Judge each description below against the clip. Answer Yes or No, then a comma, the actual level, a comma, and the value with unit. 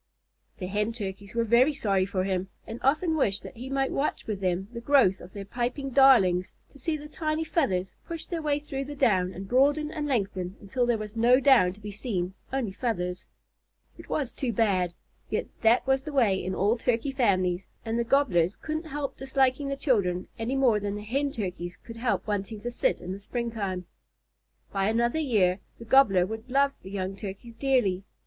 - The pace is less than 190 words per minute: No, average, 200 wpm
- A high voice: Yes, high, 230 Hz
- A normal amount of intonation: No, wide, 5.8 semitones